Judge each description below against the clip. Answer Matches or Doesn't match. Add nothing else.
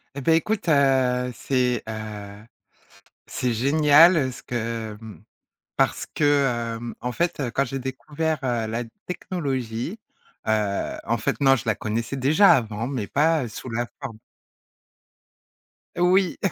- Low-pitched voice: Matches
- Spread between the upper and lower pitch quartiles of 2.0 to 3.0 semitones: Doesn't match